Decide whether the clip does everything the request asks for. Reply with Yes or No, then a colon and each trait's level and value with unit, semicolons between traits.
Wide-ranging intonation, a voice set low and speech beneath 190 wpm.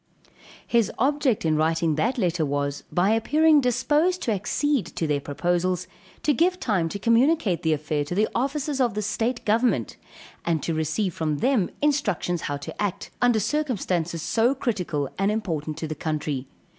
No: wide, 7.8 semitones; high, 200 Hz; average, 170 wpm